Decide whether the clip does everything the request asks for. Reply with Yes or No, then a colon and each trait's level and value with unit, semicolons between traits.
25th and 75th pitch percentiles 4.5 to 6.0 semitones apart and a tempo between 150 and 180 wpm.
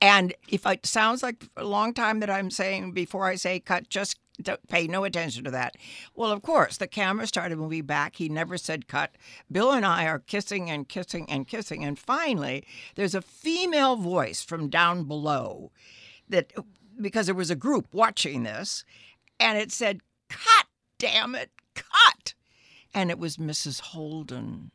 Yes: average, 4.9 semitones; average, 175 wpm